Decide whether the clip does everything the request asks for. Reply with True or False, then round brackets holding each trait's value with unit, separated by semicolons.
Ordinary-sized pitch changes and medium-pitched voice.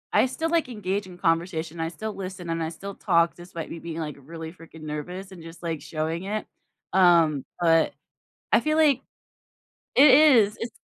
True (3.9 semitones; 175 Hz)